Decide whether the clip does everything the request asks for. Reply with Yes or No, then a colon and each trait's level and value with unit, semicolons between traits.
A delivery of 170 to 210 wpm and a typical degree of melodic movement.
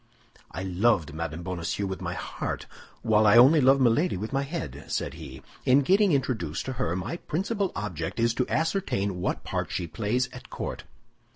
No: average, 180 wpm; wide, 7.4 semitones